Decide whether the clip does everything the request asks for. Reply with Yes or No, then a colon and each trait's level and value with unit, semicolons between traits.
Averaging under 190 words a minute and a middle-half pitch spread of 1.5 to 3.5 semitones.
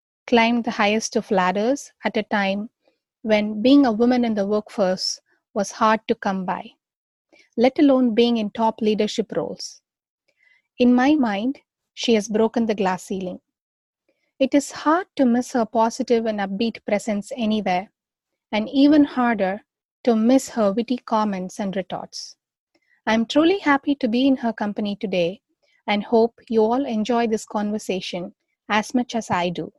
Yes: average, 160 wpm; average, 3.2 semitones